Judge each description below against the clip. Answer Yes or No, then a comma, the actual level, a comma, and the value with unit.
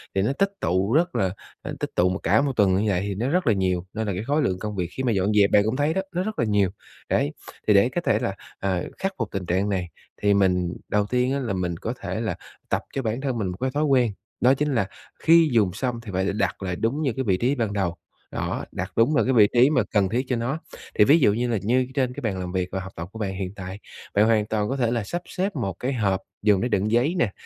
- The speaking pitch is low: Yes, low, 110 Hz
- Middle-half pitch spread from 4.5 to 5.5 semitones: Yes, average, 5.2 semitones